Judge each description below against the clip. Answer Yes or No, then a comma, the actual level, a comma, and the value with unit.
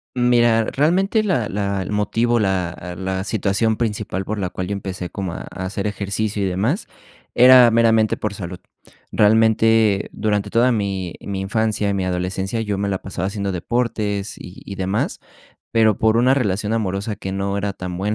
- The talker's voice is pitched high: No, low, 105 Hz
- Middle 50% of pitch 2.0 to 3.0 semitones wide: Yes, average, 2.7 semitones